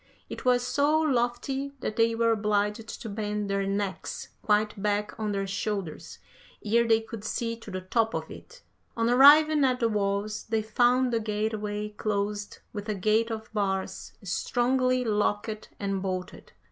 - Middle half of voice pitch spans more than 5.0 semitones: No, narrow, 2.6 semitones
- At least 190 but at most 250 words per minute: No, average, 160 wpm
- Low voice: No, high, 215 Hz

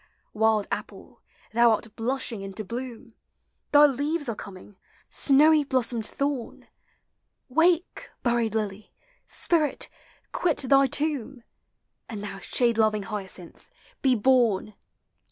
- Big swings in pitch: No, average, 4.4 semitones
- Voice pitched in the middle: No, high, 235 Hz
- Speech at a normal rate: No, slow, 110 wpm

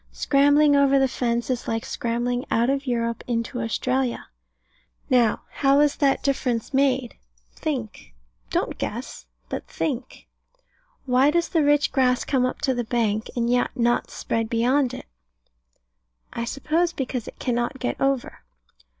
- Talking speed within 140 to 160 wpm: Yes, average, 145 wpm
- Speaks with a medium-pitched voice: No, very high, 250 Hz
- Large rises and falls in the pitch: No, average, 2.7 semitones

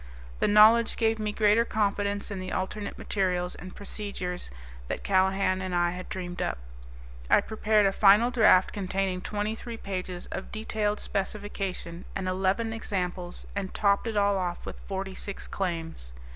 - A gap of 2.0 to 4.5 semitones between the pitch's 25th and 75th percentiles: Yes, narrow, 2.4 semitones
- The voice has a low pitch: No, high, 195 Hz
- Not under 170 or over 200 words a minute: No, average, 160 wpm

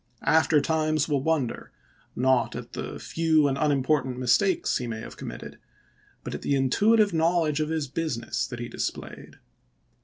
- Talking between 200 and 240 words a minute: No, average, 160 wpm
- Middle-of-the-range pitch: Yes, medium, 150 Hz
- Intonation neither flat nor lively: Yes, average, 3.8 semitones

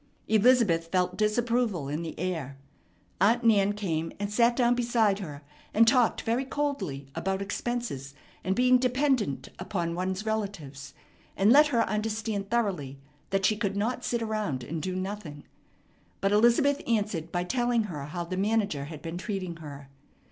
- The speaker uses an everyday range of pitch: No, wide, 5.7 semitones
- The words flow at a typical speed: Yes, average, 155 wpm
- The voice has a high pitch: Yes, high, 200 Hz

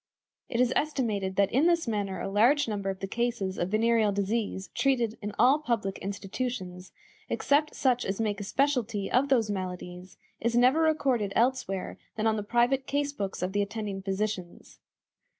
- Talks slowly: No, average, 170 wpm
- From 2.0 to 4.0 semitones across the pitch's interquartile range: No, average, 4.4 semitones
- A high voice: Yes, high, 220 Hz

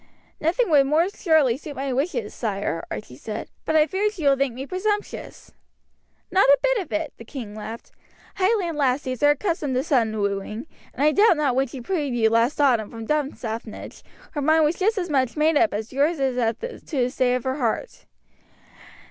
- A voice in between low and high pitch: No, very high, 275 Hz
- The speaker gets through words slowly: No, average, 200 wpm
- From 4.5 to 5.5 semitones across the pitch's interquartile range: Yes, average, 5.1 semitones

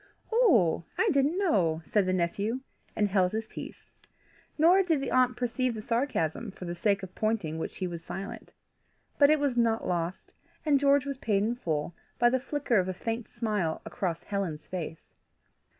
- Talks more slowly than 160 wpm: No, average, 180 wpm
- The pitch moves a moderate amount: No, wide, 6.4 semitones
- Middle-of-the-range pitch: No, high, 220 Hz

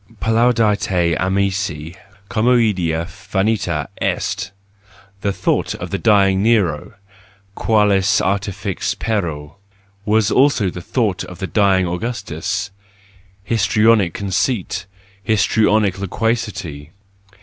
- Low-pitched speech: Yes, low, 100 Hz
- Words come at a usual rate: No, slow, 90 wpm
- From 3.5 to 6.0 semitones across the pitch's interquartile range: No, average, 3.0 semitones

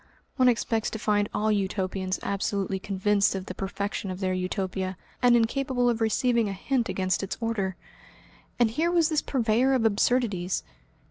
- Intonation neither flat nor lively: Yes, average, 3.9 semitones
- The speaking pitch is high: Yes, high, 210 Hz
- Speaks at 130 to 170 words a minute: Yes, average, 160 wpm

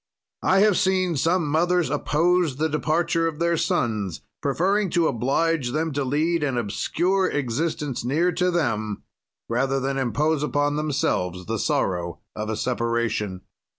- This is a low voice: No, medium, 150 Hz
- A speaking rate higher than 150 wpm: No, average, 145 wpm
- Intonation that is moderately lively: No, wide, 5.9 semitones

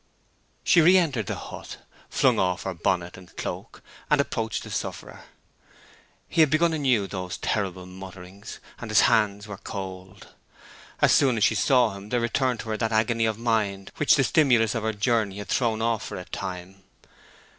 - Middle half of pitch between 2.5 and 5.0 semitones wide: Yes, average, 3.8 semitones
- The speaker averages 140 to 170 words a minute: No, average, 180 wpm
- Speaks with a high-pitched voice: No, low, 110 Hz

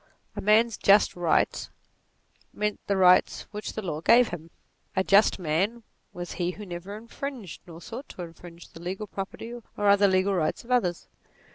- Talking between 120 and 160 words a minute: No, average, 170 wpm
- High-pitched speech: Yes, high, 195 Hz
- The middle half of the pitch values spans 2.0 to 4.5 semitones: Yes, average, 3.4 semitones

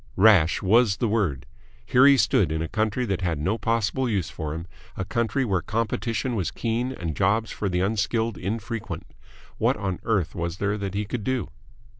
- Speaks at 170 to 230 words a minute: Yes, average, 190 wpm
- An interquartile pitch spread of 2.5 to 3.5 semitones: No, average, 4.0 semitones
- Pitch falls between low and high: No, low, 105 Hz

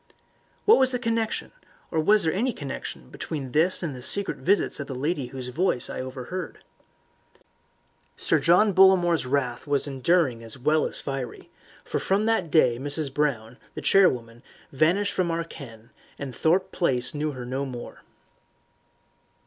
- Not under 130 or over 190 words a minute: Yes, average, 160 wpm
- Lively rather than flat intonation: Yes, wide, 6.0 semitones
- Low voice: No, medium, 150 Hz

